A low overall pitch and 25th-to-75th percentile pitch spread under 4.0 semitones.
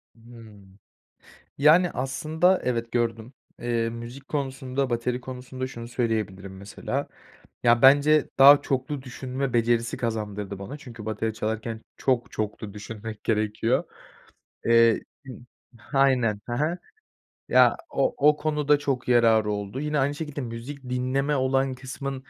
Yes: low, 125 Hz; average, 3.4 semitones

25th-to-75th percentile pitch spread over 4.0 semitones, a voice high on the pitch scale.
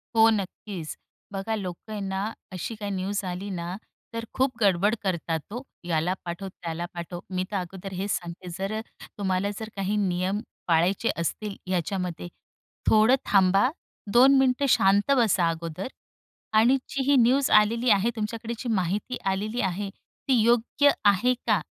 No: average, 3.6 semitones; high, 200 Hz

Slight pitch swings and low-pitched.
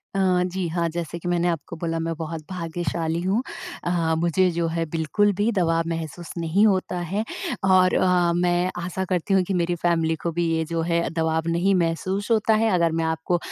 No: narrow, 1.9 semitones; medium, 170 Hz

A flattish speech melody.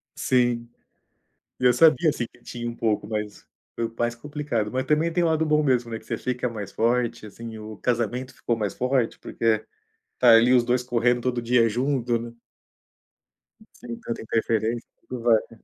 Yes: narrow, 1.7 semitones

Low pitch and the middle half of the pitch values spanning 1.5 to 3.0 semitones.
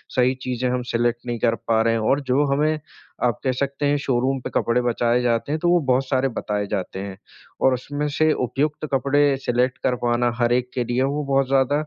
Yes: low, 125 Hz; narrow, 2.6 semitones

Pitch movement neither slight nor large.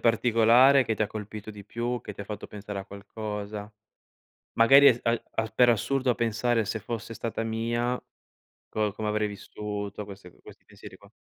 No: narrow, 2.2 semitones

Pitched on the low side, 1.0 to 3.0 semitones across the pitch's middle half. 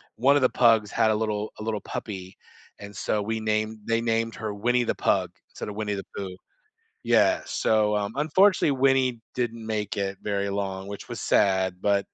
Yes: low, 110 Hz; narrow, 2.4 semitones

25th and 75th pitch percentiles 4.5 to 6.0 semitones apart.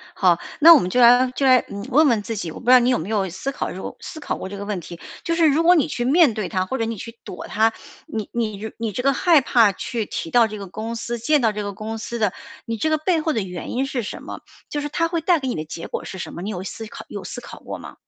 Yes: average, 5.1 semitones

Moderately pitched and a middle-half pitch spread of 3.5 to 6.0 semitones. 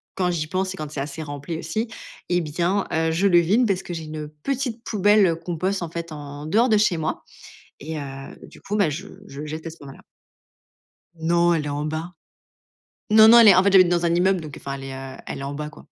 Yes: medium, 170 Hz; average, 4.0 semitones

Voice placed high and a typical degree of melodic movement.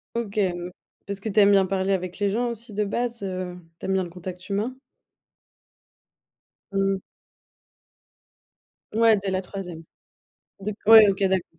No: high, 195 Hz; narrow, 2.3 semitones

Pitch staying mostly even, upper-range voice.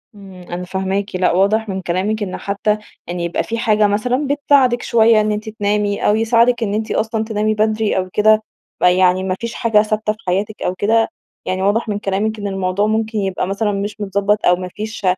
Yes: narrow, 2.3 semitones; high, 210 Hz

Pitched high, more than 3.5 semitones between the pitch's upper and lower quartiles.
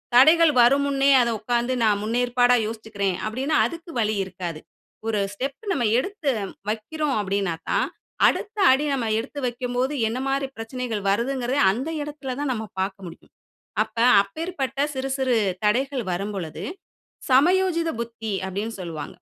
Yes: high, 245 Hz; average, 4.5 semitones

